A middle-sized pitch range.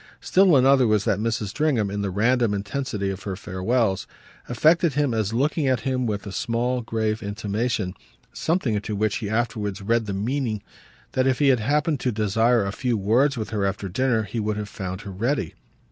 Yes: average, 4.0 semitones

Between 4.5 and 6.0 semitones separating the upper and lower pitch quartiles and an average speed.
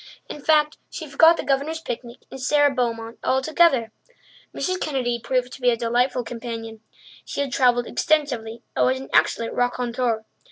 No: average, 3.3 semitones; average, 160 wpm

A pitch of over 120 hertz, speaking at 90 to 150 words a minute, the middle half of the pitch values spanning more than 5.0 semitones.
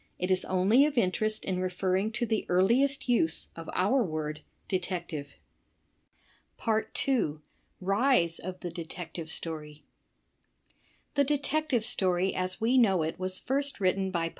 Yes: medium, 185 Hz; average, 140 wpm; wide, 5.5 semitones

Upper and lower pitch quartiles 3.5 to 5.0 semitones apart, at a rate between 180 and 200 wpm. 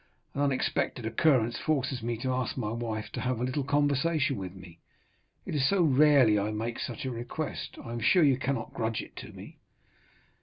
Yes: average, 4.0 semitones; average, 195 wpm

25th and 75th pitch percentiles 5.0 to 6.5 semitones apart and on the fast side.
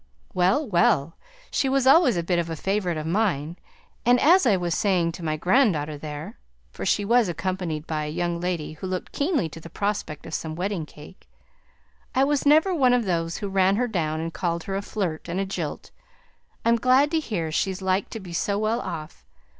Yes: average, 5.3 semitones; fast, 210 wpm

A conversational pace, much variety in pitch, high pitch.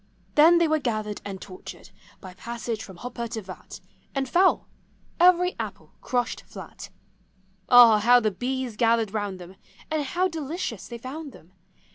Yes: average, 160 wpm; wide, 6.0 semitones; high, 240 Hz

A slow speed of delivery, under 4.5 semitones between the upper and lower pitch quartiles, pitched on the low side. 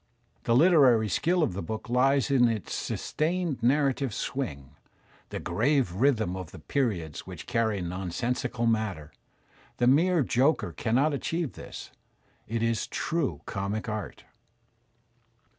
No: slow, 130 wpm; average, 5.1 semitones; low, 120 Hz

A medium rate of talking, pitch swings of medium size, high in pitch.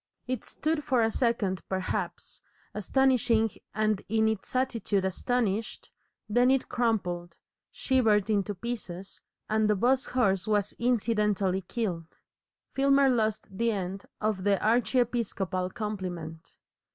No: slow, 115 wpm; average, 4.0 semitones; high, 215 Hz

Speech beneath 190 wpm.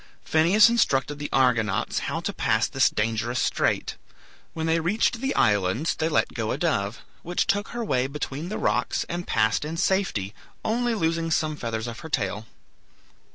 Yes: average, 170 wpm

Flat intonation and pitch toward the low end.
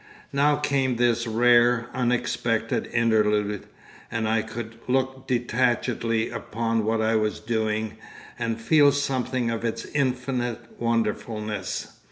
Yes: narrow, 2.1 semitones; low, 115 Hz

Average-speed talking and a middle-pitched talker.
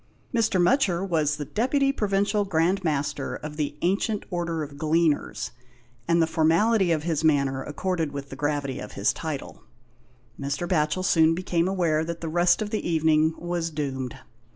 Yes: average, 165 wpm; medium, 165 Hz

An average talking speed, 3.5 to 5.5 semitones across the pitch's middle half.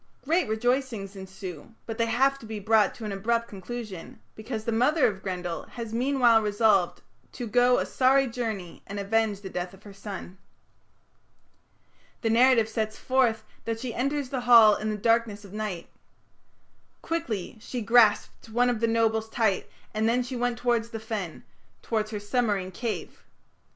No: average, 165 wpm; average, 2.9 semitones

